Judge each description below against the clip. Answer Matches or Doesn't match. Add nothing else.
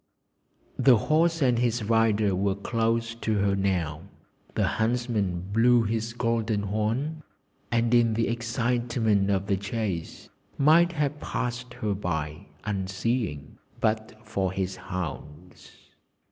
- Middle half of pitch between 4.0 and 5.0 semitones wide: Doesn't match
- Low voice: Matches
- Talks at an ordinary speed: Doesn't match